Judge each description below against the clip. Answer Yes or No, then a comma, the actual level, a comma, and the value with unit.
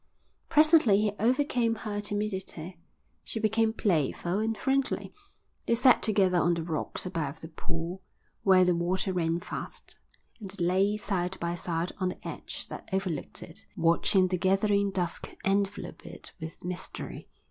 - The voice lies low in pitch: No, high, 190 Hz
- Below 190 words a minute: Yes, average, 150 wpm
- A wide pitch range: No, average, 3.4 semitones